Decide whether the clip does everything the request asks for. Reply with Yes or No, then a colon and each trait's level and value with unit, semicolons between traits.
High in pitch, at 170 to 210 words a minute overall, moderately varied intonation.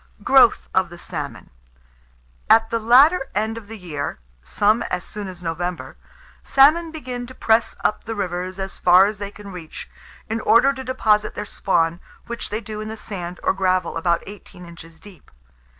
Yes: high, 205 Hz; average, 180 wpm; average, 4.2 semitones